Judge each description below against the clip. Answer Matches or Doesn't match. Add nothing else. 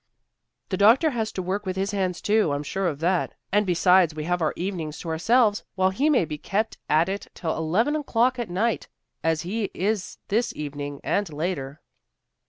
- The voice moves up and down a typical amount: Matches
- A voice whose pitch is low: Doesn't match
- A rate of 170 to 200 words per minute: Matches